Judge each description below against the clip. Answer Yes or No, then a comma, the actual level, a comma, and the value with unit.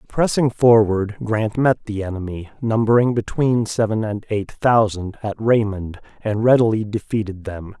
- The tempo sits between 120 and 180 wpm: Yes, average, 140 wpm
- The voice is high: No, low, 110 Hz